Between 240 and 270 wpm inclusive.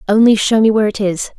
Yes: fast, 260 wpm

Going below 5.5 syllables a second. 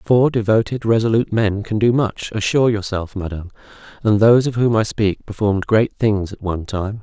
No: 5.7 syllables/s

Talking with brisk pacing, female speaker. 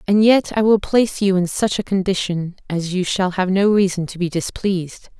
Yes: fast, 220 wpm; female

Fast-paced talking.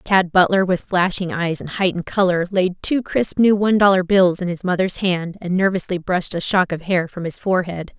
Yes: fast, 220 wpm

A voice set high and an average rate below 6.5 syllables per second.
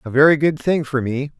No: medium, 140 Hz; 5.7 syllables/s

